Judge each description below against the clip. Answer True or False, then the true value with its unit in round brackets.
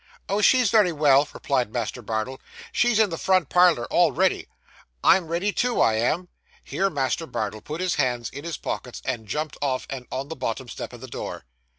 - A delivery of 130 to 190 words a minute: False (200 wpm)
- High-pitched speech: False (145 Hz)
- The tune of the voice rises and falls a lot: True (6.7 semitones)